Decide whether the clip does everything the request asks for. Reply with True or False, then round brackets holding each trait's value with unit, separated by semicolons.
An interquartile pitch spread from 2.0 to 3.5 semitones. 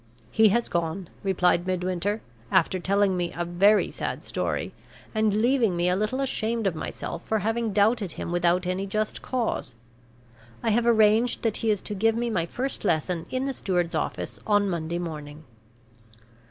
False (4.1 semitones)